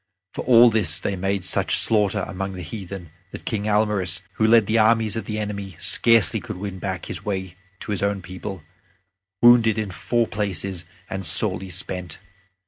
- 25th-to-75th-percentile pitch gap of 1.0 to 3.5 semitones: Yes, average, 2.7 semitones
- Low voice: Yes, low, 100 Hz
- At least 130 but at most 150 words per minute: No, average, 175 wpm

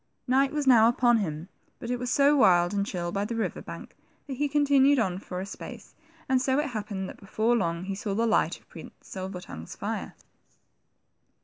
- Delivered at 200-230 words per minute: Yes, fast, 205 wpm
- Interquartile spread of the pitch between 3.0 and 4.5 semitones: No, wide, 5.5 semitones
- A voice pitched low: No, high, 225 Hz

